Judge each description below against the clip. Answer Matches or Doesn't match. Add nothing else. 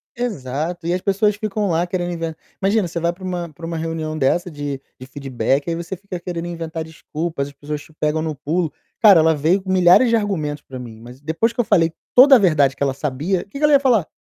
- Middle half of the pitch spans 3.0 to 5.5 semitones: Matches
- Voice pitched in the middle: Matches